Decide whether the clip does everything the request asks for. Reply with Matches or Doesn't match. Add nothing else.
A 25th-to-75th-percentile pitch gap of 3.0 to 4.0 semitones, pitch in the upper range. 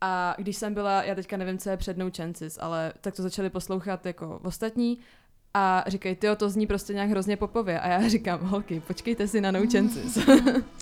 Doesn't match